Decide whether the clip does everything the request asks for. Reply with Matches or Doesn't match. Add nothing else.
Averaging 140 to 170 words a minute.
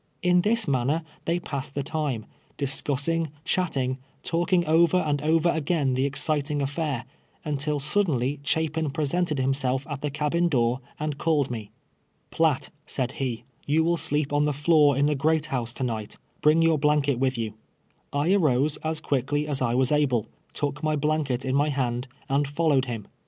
Doesn't match